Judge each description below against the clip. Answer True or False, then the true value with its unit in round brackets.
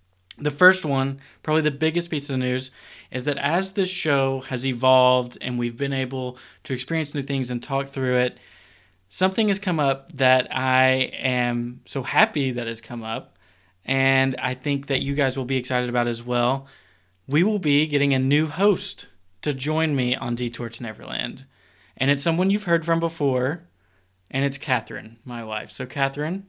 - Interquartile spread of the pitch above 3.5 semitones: False (3.1 semitones)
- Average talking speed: True (185 wpm)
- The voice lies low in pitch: True (130 Hz)